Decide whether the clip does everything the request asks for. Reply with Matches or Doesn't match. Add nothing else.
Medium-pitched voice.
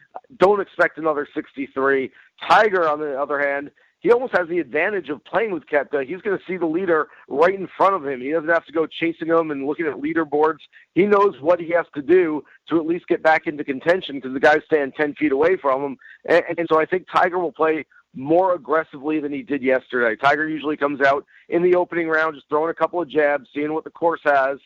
Matches